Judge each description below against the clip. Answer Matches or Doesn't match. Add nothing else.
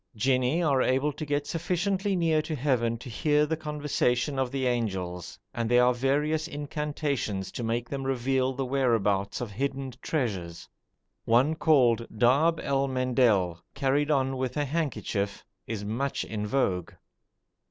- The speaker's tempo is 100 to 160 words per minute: Matches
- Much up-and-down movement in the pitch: Doesn't match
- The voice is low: Matches